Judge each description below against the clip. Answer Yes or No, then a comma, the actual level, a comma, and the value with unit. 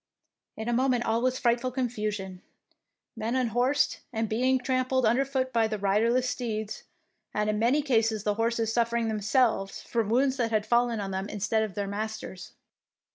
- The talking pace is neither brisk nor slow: Yes, average, 185 wpm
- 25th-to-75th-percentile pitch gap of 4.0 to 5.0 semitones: No, average, 2.8 semitones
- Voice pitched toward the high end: Yes, high, 230 Hz